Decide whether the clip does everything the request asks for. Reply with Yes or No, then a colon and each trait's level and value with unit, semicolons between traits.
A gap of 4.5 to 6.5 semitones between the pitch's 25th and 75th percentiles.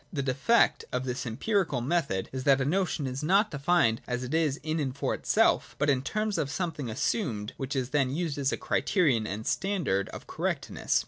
Yes: average, 5.1 semitones